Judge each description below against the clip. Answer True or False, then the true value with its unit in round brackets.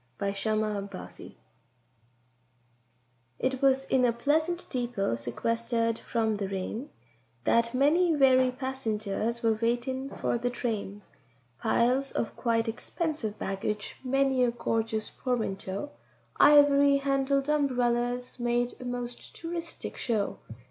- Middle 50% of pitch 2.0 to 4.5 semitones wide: True (3.5 semitones)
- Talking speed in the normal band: False (115 wpm)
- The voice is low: False (240 Hz)